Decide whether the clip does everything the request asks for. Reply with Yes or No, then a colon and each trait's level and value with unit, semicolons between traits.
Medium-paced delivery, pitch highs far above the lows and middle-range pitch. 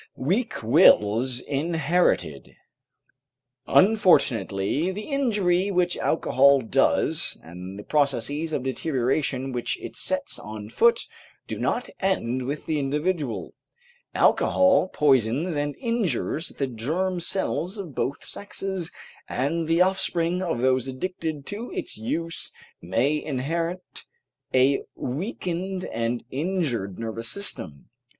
No: slow, 110 wpm; wide, 6.4 semitones; medium, 150 Hz